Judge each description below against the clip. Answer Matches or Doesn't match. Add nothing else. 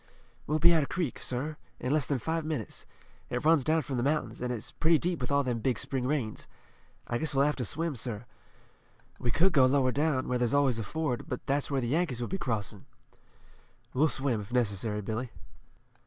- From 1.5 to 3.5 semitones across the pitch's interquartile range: Doesn't match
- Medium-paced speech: Doesn't match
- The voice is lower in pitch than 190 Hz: Matches